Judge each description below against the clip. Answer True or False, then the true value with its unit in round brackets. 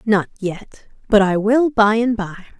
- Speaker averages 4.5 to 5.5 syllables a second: False (4.1 syllables/s)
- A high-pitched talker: True (210 Hz)